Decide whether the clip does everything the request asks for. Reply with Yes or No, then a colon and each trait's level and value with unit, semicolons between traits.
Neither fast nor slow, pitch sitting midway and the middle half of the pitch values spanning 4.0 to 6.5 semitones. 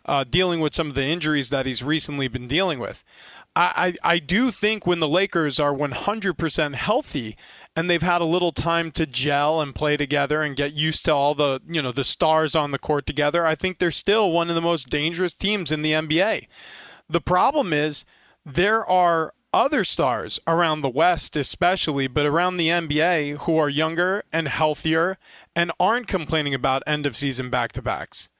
No: average, 195 wpm; medium, 160 Hz; average, 3.1 semitones